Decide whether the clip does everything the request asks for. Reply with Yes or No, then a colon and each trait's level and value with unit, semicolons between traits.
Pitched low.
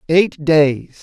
No: medium, 155 Hz